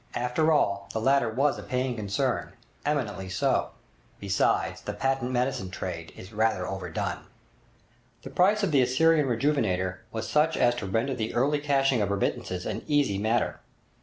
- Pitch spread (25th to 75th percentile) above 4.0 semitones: Yes, wide, 5.6 semitones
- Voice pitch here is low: Yes, low, 120 Hz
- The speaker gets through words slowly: No, average, 155 wpm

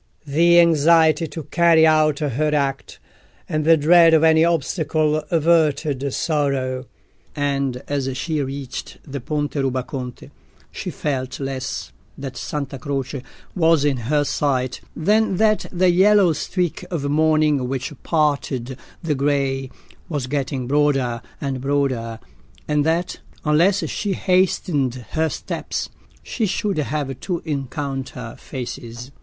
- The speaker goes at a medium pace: No, slow, 125 wpm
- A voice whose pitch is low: No, medium, 145 Hz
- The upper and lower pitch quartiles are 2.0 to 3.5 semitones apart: Yes, average, 3.1 semitones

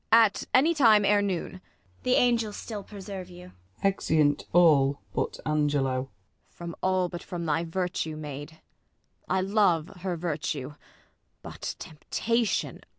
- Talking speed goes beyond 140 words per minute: No, slow, 135 wpm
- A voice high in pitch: No, medium, 180 Hz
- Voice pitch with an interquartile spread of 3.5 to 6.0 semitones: Yes, average, 4.8 semitones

